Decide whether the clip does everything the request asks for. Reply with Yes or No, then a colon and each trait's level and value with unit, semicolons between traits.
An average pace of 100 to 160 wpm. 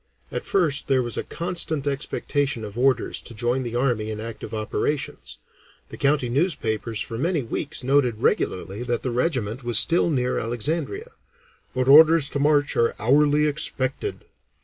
Yes: average, 155 wpm